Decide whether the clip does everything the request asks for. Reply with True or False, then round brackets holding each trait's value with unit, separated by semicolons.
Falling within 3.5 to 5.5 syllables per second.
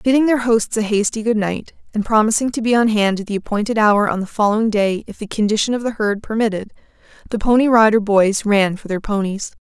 False (5.9 syllables/s)